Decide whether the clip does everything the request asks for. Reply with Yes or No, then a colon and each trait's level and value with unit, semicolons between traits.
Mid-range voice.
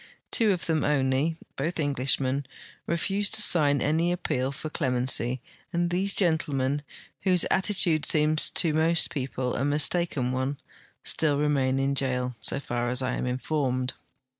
Yes: medium, 145 Hz